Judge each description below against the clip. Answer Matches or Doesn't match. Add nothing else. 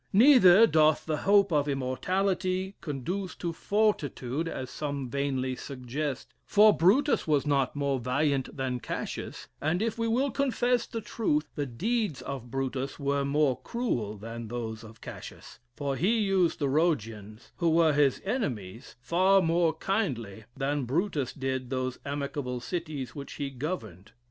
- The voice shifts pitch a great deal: Matches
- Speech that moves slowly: Doesn't match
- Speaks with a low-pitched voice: Doesn't match